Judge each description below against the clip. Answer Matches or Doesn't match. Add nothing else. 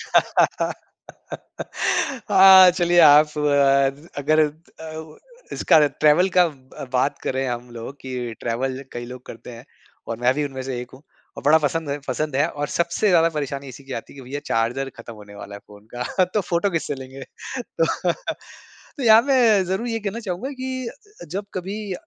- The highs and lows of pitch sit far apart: Matches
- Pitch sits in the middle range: Matches